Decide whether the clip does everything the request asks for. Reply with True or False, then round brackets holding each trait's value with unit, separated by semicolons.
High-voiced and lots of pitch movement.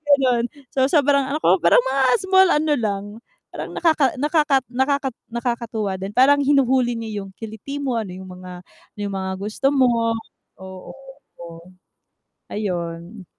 True (235 Hz; 6.0 semitones)